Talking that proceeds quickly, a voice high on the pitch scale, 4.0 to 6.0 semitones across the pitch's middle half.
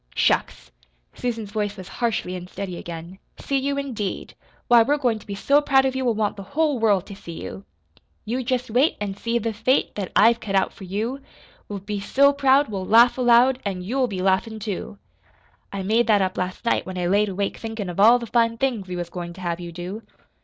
Yes: fast, 220 wpm; high, 215 Hz; average, 4.3 semitones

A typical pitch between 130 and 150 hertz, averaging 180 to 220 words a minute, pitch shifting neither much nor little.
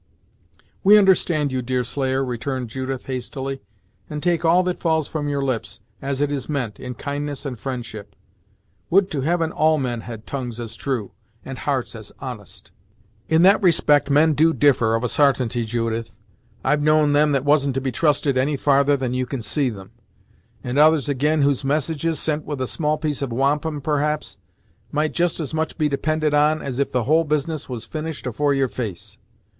Yes: medium, 140 Hz; average, 185 wpm; average, 3.2 semitones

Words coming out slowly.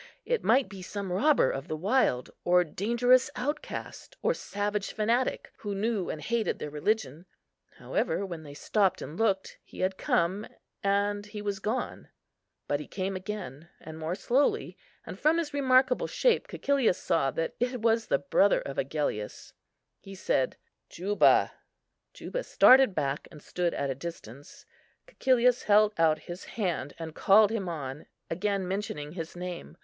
No: average, 155 wpm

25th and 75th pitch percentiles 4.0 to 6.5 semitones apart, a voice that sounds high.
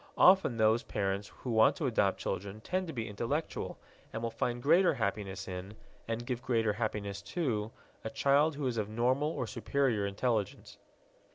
No: average, 4.4 semitones; low, 115 Hz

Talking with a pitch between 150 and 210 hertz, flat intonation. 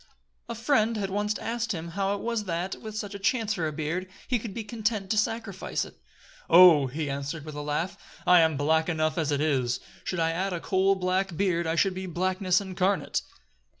No: medium, 185 Hz; average, 4.1 semitones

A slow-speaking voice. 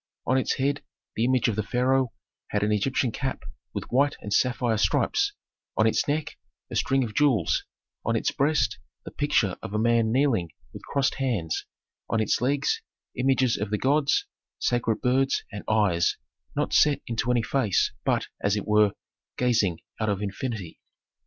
No: average, 170 wpm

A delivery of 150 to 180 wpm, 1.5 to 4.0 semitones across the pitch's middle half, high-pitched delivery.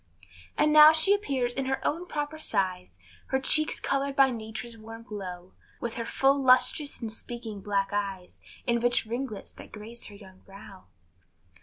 No: average, 165 wpm; average, 4.9 semitones; high, 235 Hz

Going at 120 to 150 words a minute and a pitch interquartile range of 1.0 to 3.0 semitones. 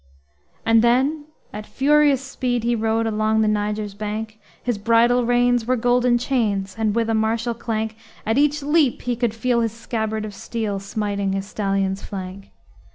No: average, 165 wpm; narrow, 2.5 semitones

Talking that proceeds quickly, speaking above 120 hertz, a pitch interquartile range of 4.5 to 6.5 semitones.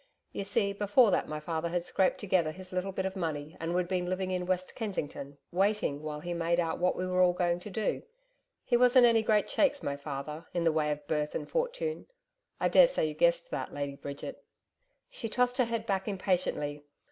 Yes: fast, 210 wpm; medium, 185 Hz; average, 5.1 semitones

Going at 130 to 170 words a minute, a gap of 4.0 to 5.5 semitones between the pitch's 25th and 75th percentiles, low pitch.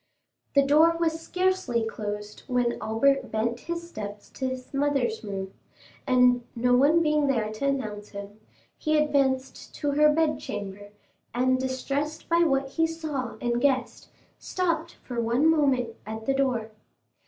No: average, 145 wpm; average, 4.8 semitones; very high, 260 Hz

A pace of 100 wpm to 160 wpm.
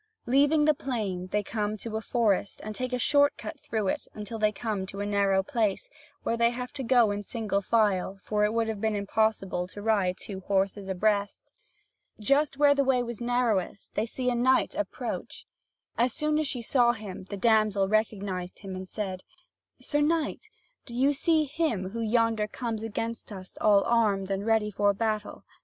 No: average, 190 wpm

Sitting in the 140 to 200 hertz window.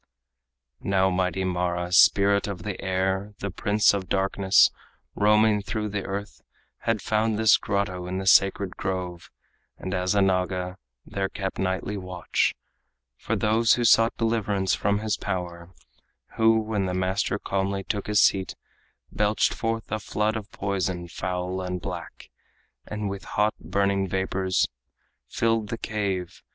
No: low, 100 Hz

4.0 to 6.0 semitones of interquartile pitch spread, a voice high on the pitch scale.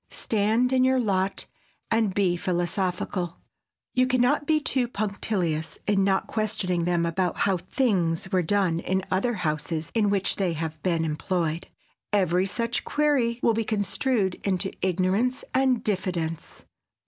Yes: average, 4.4 semitones; high, 195 Hz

